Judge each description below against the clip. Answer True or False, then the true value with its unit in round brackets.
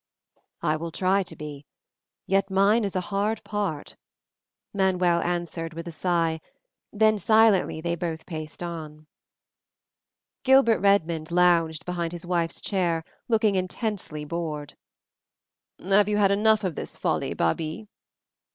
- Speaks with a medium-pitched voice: True (175 Hz)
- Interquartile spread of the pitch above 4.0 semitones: False (3.5 semitones)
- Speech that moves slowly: True (130 wpm)